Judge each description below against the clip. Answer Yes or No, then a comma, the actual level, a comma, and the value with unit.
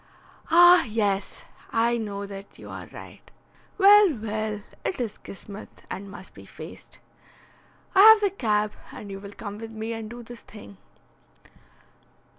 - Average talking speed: Yes, average, 150 wpm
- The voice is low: No, high, 220 Hz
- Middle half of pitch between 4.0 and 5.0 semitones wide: No, average, 3.1 semitones